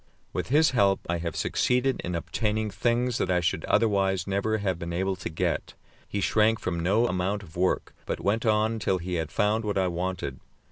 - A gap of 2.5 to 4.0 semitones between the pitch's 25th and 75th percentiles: Yes, average, 3.3 semitones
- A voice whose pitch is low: Yes, low, 100 Hz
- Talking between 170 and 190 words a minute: No, average, 200 wpm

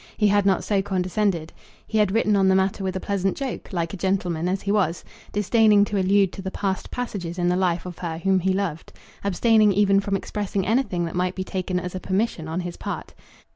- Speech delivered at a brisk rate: Yes, fast, 225 wpm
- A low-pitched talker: No, high, 190 Hz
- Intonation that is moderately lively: No, narrow, 2.1 semitones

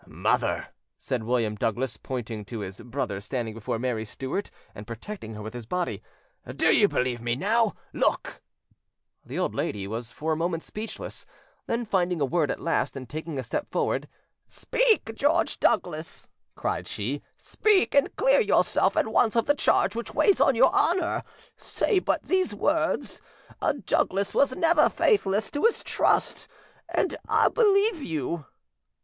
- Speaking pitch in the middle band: Yes, medium, 165 Hz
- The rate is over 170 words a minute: No, average, 160 wpm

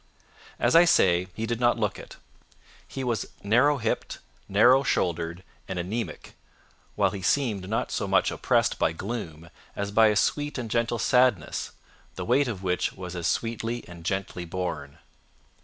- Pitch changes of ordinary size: Yes, average, 5.0 semitones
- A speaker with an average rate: Yes, average, 160 wpm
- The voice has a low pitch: Yes, low, 105 Hz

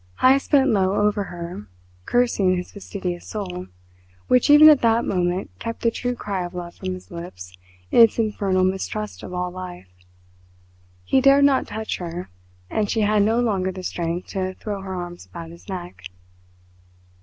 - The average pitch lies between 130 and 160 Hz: No, high, 190 Hz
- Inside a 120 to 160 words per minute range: No, average, 170 wpm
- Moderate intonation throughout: Yes, average, 3.9 semitones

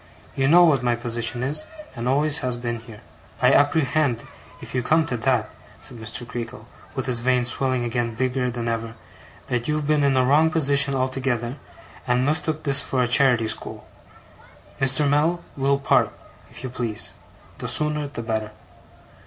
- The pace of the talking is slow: No, average, 170 wpm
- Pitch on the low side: Yes, low, 130 Hz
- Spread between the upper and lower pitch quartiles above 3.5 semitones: No, average, 3.1 semitones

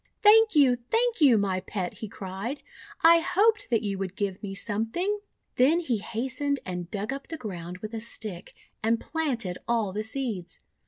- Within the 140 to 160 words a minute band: No, average, 180 wpm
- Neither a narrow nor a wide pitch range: No, wide, 7.0 semitones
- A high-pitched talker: Yes, high, 230 Hz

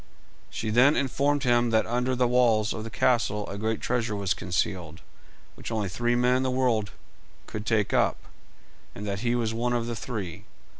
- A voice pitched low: Yes, low, 115 Hz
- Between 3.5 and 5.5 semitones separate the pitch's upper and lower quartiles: No, average, 2.8 semitones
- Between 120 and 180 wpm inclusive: No, average, 195 wpm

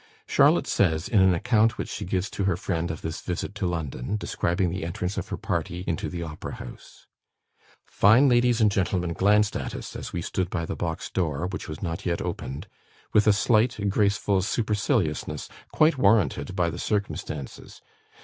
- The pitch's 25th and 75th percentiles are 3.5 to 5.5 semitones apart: Yes, average, 3.8 semitones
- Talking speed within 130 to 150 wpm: No, average, 180 wpm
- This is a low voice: Yes, very low, 95 Hz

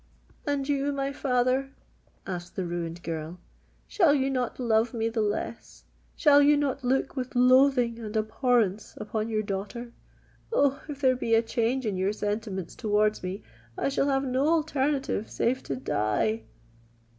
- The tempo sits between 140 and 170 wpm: Yes, average, 155 wpm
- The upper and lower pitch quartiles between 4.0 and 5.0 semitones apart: Yes, average, 4.5 semitones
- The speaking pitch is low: No, high, 240 Hz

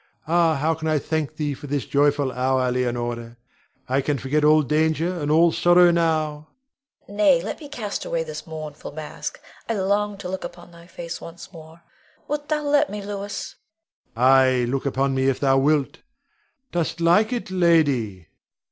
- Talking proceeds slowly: No, average, 175 wpm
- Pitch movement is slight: No, average, 4.5 semitones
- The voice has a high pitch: No, medium, 160 Hz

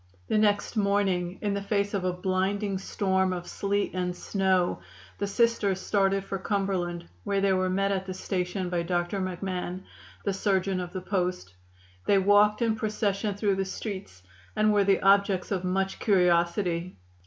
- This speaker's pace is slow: No, average, 165 wpm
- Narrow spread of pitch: Yes, narrow, 1.7 semitones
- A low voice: No, high, 195 Hz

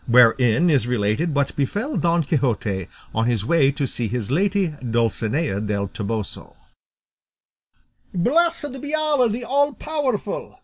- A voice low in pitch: No, medium, 145 Hz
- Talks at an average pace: No, slow, 130 wpm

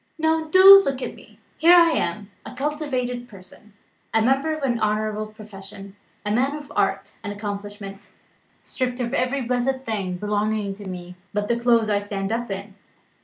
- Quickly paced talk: No, average, 170 wpm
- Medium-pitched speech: No, high, 220 Hz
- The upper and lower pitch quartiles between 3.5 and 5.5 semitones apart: Yes, average, 4.6 semitones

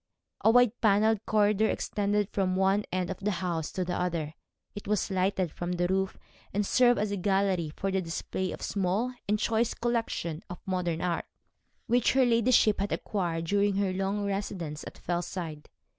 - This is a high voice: Yes, high, 195 Hz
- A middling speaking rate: Yes, average, 180 wpm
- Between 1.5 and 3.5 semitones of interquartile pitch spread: Yes, average, 2.7 semitones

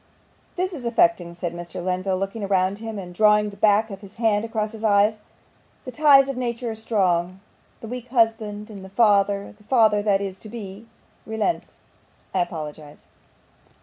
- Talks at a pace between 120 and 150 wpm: No, average, 180 wpm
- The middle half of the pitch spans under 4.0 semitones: Yes, average, 2.9 semitones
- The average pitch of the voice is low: No, high, 210 Hz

